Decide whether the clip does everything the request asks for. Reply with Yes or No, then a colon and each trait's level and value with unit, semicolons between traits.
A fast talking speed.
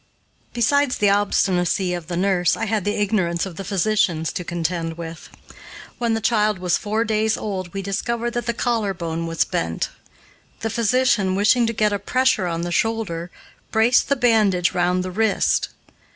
No: average, 170 wpm